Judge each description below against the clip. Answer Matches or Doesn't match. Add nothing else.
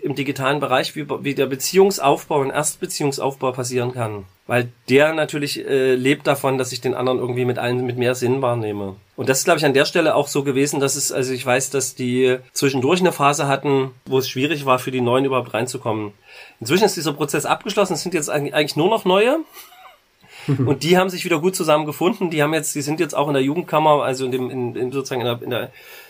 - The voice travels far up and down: Doesn't match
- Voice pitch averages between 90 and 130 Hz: Doesn't match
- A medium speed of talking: Doesn't match